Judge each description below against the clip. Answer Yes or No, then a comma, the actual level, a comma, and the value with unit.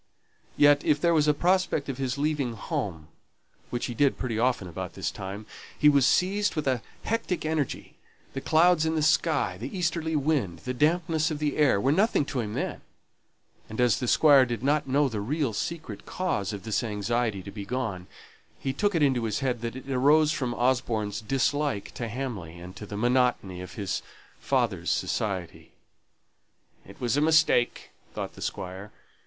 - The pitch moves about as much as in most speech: No, wide, 5.8 semitones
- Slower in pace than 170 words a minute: No, average, 180 wpm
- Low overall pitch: Yes, low, 130 Hz